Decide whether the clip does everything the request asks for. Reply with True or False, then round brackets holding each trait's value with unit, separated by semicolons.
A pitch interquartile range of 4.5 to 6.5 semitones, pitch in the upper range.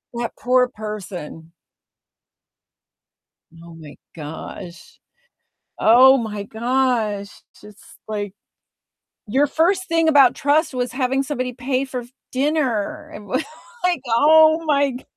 True (5.2 semitones; 250 Hz)